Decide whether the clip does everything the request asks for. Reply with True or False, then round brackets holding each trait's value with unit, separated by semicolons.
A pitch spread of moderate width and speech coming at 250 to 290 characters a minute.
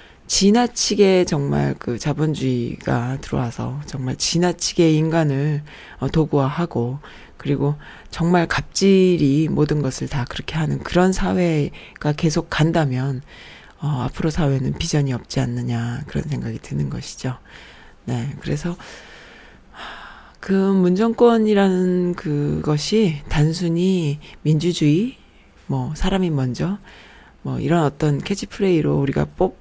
True (4.7 semitones; 255 characters per minute)